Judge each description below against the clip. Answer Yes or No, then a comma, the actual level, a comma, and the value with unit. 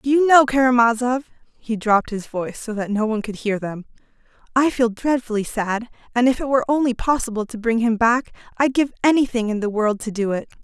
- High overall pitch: Yes, high, 235 Hz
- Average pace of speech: No, fast, 215 wpm